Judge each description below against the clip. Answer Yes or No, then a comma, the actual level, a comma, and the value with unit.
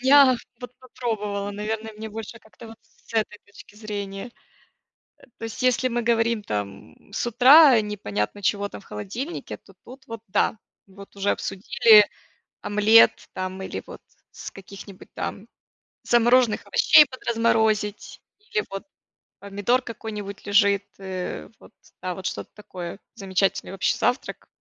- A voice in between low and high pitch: No, high, 210 Hz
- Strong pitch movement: No, average, 2.9 semitones